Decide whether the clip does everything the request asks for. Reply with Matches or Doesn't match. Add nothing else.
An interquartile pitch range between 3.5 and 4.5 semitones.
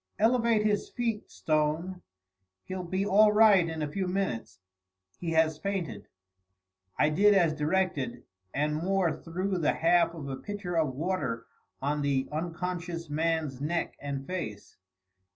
Matches